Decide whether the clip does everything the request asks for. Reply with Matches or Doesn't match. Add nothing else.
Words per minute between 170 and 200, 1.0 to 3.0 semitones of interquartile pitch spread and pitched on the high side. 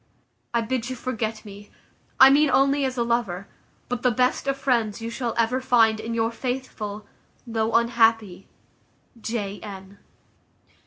Doesn't match